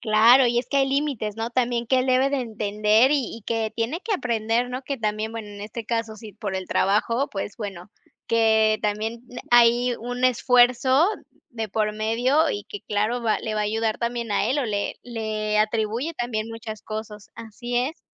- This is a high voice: Yes, high, 230 Hz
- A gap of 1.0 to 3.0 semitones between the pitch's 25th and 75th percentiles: Yes, narrow, 2.5 semitones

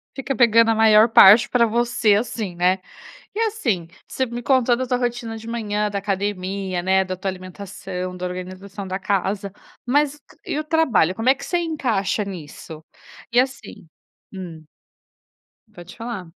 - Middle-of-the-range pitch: No, high, 210 Hz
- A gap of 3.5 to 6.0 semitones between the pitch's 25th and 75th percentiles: Yes, average, 4.4 semitones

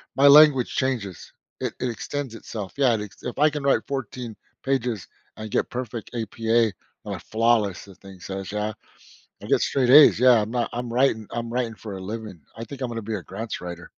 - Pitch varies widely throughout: No, average, 3.4 semitones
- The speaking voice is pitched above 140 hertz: No, low, 115 Hz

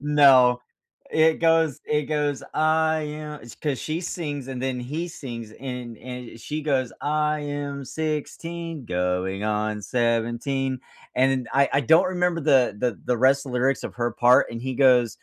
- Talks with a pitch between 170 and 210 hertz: No, low, 135 Hz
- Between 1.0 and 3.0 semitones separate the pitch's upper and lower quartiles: No, average, 3.7 semitones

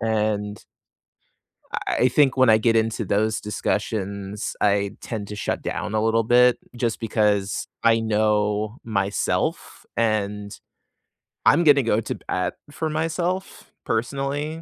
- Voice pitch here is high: No, low, 110 Hz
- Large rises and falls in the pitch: No, average, 3.1 semitones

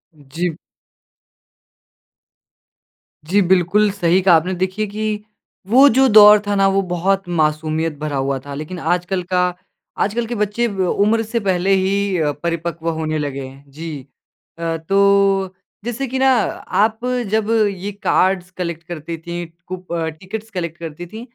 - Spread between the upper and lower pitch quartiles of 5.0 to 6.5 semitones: No, average, 3.8 semitones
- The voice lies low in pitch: No, medium, 185 Hz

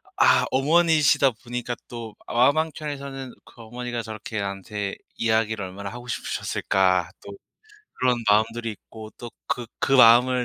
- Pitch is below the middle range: Yes, low, 120 Hz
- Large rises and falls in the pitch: No, average, 3.1 semitones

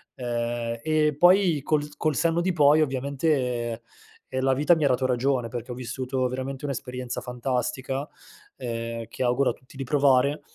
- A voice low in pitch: Yes, low, 130 Hz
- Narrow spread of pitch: No, average, 3.0 semitones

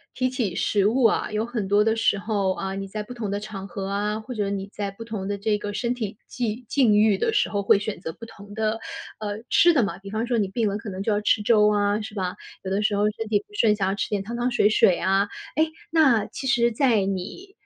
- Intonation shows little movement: Yes, narrow, 2.2 semitones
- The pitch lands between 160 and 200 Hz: No, high, 210 Hz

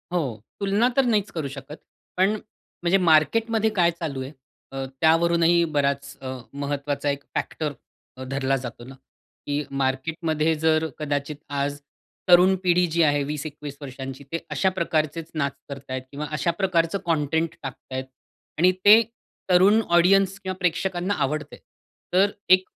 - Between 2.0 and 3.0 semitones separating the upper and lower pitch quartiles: No, average, 4.2 semitones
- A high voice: No, medium, 155 Hz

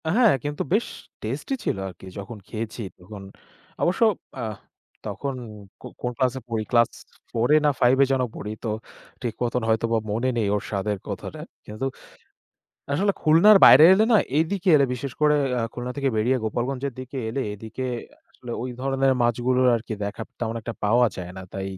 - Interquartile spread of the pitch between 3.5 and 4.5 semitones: Yes, average, 3.8 semitones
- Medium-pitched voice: No, low, 125 Hz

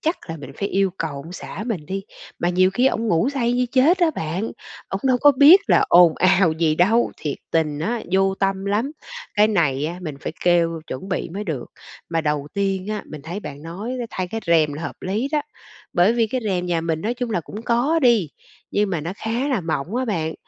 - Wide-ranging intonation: Yes, wide, 5.9 semitones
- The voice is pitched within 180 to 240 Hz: Yes, high, 190 Hz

